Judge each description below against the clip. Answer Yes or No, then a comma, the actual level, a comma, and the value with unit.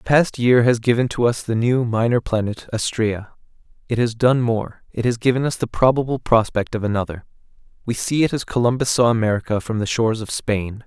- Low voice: Yes, low, 115 Hz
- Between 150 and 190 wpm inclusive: No, average, 200 wpm